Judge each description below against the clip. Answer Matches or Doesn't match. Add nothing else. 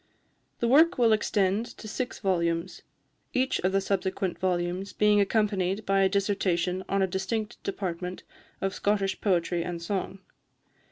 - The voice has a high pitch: Matches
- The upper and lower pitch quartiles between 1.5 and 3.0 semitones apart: Matches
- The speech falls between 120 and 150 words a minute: Matches